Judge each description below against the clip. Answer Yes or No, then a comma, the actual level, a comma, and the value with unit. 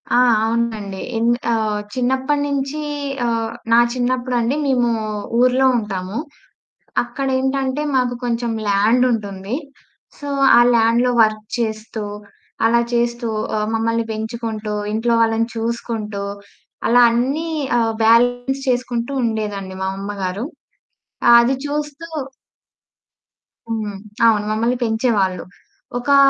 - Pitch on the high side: Yes, high, 230 Hz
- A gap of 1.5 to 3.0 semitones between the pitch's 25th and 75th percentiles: Yes, narrow, 2.4 semitones